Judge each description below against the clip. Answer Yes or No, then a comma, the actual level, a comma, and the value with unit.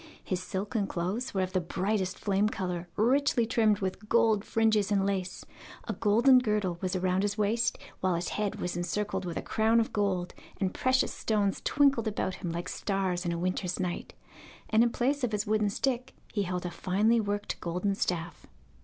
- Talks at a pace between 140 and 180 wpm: No, average, 190 wpm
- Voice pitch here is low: No, high, 200 Hz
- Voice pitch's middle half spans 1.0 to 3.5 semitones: Yes, average, 3.1 semitones